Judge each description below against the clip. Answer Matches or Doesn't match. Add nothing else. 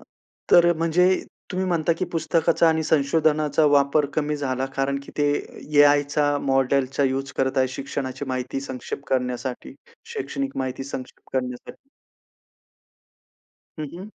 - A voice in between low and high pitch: Matches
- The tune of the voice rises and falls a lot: Doesn't match